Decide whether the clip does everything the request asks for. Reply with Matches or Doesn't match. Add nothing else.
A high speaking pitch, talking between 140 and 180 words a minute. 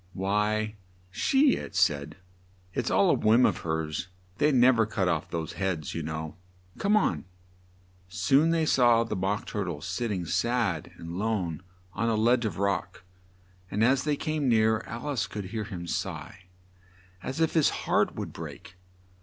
Doesn't match